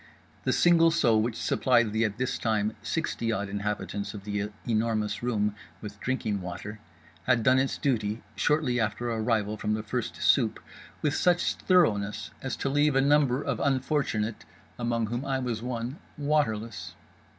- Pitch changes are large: No, average, 4.0 semitones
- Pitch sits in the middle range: No, low, 115 Hz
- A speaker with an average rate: Yes, average, 160 wpm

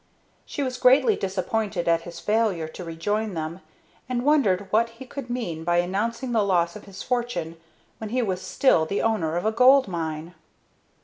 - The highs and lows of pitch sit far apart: Yes, wide, 5.7 semitones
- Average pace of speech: Yes, average, 180 wpm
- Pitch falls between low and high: No, high, 205 Hz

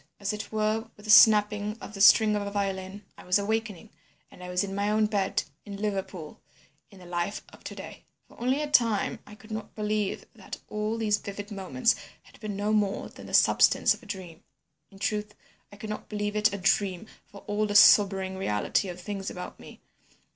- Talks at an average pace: No, fast, 210 wpm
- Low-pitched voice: No, high, 205 Hz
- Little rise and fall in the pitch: Yes, narrow, 1.6 semitones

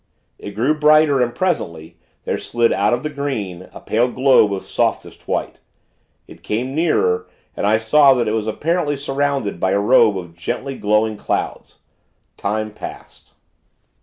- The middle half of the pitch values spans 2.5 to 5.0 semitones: No, wide, 5.4 semitones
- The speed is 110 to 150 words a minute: No, average, 160 wpm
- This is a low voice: Yes, low, 120 Hz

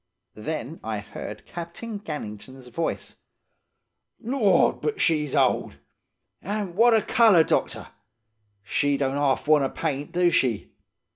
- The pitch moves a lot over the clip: Yes, wide, 7.0 semitones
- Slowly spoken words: Yes, slow, 125 wpm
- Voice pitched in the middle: Yes, medium, 160 Hz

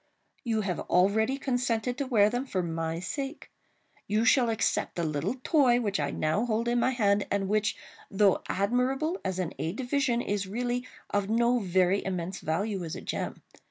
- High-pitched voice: Yes, high, 215 Hz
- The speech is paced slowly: No, average, 185 wpm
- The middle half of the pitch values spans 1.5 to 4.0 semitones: No, average, 4.6 semitones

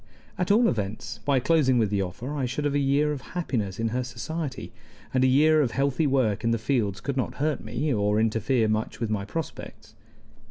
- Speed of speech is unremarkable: No, fast, 210 wpm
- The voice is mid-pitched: No, low, 130 Hz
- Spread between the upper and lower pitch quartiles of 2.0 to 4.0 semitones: No, average, 4.6 semitones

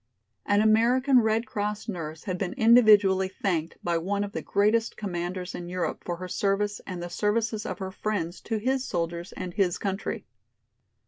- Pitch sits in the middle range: No, high, 200 Hz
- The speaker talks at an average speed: Yes, average, 175 wpm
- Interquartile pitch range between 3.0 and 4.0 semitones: Yes, average, 3.5 semitones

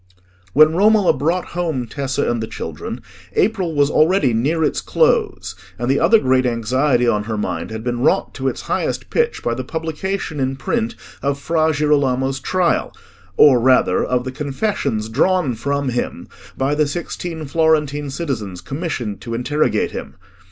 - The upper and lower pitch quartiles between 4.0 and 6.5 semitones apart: Yes, average, 4.6 semitones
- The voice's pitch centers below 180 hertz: Yes, medium, 140 Hz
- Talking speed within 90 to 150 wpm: No, average, 160 wpm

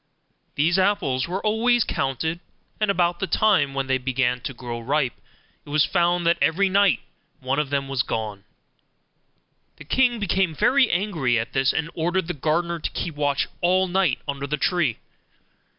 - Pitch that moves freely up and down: Yes, wide, 5.7 semitones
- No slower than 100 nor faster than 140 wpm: No, average, 170 wpm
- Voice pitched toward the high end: No, medium, 160 Hz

